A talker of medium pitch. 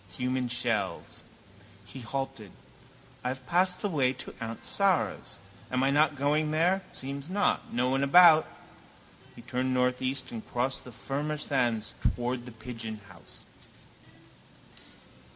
No: low, 130 Hz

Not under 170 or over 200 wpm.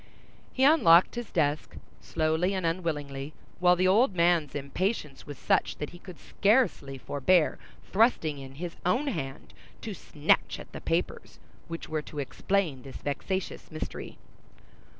No: average, 145 wpm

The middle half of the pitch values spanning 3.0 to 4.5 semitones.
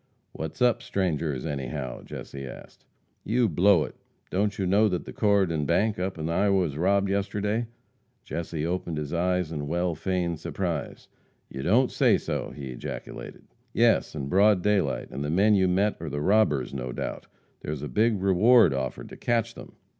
No: wide, 5.4 semitones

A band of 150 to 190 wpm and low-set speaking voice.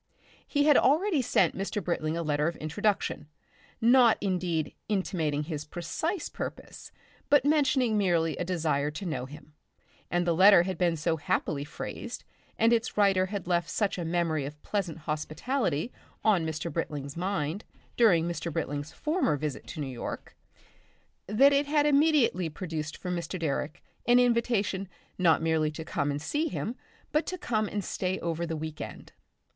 No: average, 165 wpm; medium, 175 Hz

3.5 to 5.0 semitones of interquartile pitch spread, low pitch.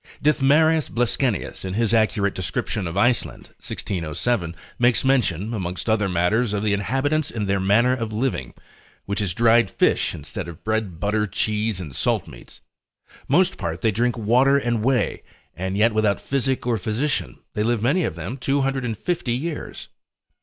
Yes: average, 4.4 semitones; low, 110 Hz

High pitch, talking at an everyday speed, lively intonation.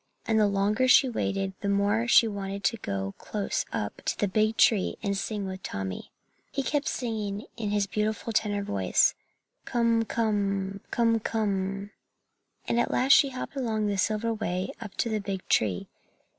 No: high, 210 Hz; average, 170 wpm; narrow, 2.4 semitones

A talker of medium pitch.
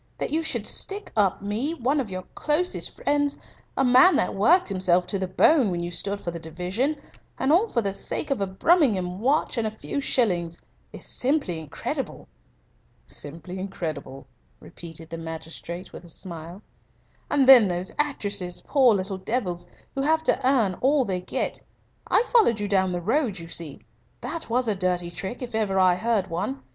No: high, 200 Hz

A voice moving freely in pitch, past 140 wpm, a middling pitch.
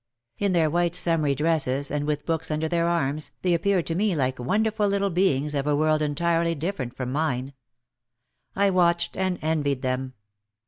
No: average, 3.5 semitones; average, 175 wpm; medium, 160 Hz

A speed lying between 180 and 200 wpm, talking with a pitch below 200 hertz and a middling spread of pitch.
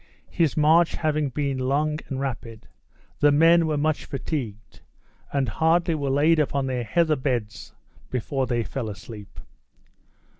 No: average, 140 wpm; medium, 140 Hz; average, 3.5 semitones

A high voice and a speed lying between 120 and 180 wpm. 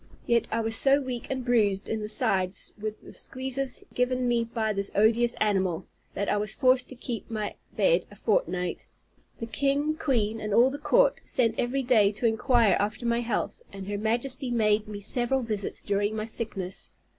No: high, 230 Hz; average, 190 wpm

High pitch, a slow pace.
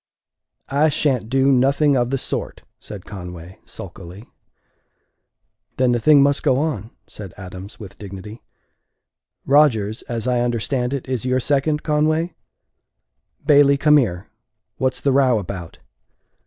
No: low, 125 Hz; slow, 130 wpm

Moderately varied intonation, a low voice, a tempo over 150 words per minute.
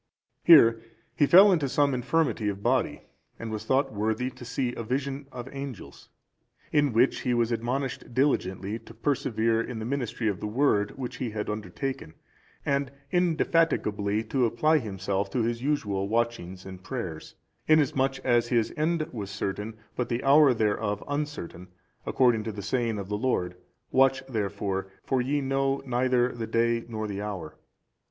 Yes: average, 4.3 semitones; low, 120 Hz; average, 160 wpm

